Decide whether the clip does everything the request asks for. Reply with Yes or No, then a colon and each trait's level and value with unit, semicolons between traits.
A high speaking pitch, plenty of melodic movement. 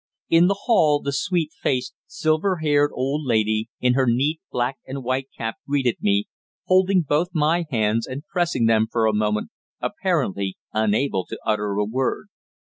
No: low, 130 Hz; wide, 5.8 semitones